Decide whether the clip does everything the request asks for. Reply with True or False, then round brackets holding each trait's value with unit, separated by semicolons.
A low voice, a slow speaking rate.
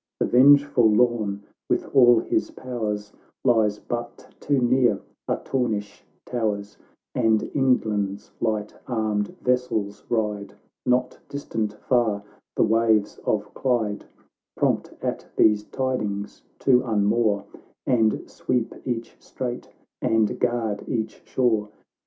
True (110 Hz; 110 wpm)